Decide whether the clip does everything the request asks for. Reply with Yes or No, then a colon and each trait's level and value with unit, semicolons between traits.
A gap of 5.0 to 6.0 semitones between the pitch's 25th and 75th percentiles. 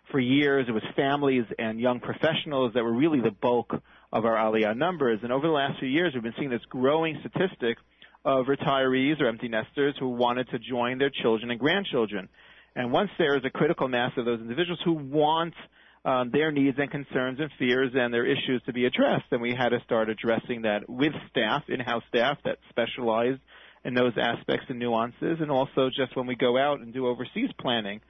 No: average, 2.8 semitones